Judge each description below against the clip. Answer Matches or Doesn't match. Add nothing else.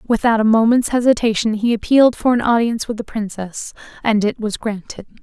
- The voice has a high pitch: Matches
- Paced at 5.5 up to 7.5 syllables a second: Matches